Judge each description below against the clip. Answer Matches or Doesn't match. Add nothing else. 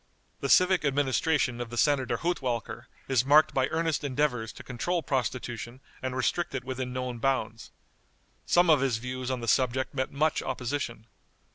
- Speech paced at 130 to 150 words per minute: Doesn't match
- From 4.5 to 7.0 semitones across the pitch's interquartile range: Doesn't match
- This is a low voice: Matches